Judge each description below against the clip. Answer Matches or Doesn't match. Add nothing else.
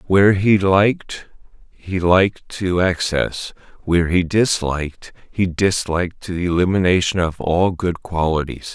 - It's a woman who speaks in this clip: Doesn't match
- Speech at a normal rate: Doesn't match